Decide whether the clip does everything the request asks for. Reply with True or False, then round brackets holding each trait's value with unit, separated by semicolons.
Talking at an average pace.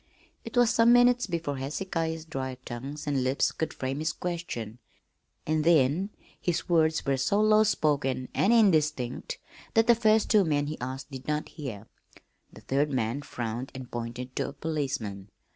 True (165 wpm)